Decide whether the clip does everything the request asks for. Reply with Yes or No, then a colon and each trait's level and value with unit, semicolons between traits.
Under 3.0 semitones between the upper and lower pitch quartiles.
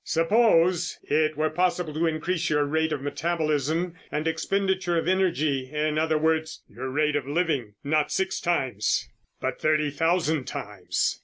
Yes: narrow, 2.6 semitones